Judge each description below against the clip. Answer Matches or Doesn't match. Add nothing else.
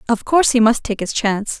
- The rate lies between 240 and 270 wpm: Matches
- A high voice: Matches